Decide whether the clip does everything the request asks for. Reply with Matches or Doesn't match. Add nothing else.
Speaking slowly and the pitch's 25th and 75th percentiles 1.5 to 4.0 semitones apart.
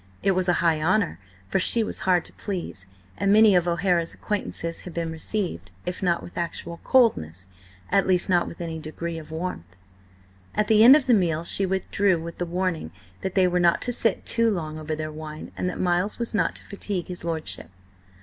Doesn't match